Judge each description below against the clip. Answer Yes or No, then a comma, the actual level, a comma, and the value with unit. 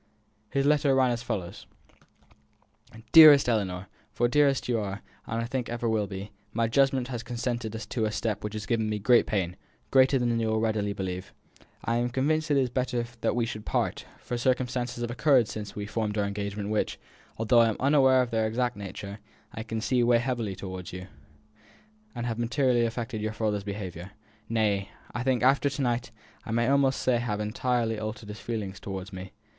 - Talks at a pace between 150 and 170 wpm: No, average, 195 wpm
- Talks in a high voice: No, low, 115 Hz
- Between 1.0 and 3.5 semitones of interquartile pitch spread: Yes, average, 3.0 semitones